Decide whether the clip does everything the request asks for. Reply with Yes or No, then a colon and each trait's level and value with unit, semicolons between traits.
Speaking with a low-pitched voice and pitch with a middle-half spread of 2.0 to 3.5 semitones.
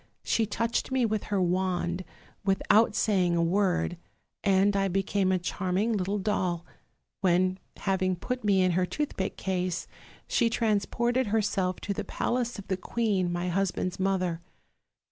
No: high, 195 Hz; narrow, 2.4 semitones